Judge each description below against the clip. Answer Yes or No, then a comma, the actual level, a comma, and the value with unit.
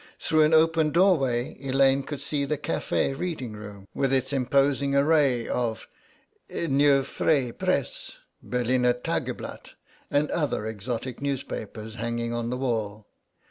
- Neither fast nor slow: No, slow, 130 wpm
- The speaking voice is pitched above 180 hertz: No, low, 135 Hz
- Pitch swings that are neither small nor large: Yes, average, 3.3 semitones